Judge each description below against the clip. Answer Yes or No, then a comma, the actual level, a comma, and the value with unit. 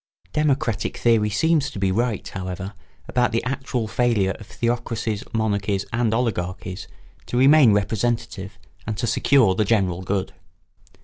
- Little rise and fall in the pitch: No, average, 3.6 semitones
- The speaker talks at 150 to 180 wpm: No, average, 140 wpm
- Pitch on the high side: No, low, 110 Hz